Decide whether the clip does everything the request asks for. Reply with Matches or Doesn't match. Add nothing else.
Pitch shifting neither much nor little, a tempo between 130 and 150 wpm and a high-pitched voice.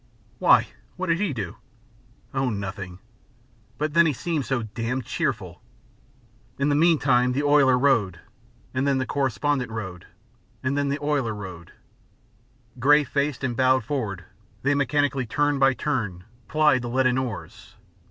Doesn't match